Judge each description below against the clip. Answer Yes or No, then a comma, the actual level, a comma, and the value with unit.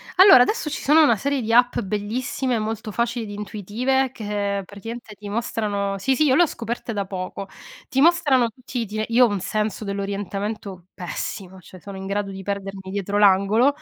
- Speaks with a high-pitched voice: Yes, high, 210 Hz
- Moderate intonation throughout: Yes, average, 3.7 semitones